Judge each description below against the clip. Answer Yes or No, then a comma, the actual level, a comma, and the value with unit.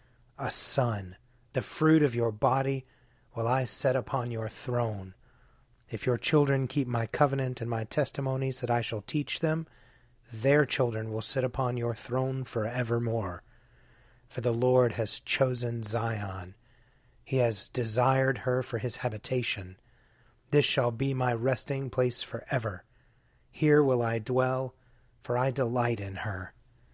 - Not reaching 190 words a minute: Yes, average, 145 wpm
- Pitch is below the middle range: Yes, low, 125 Hz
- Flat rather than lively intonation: Yes, narrow, 2.0 semitones